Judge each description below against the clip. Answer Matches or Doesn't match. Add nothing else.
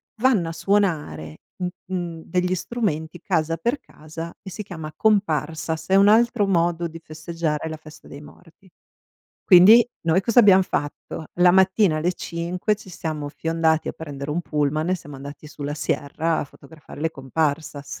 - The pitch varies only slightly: Doesn't match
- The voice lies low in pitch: Doesn't match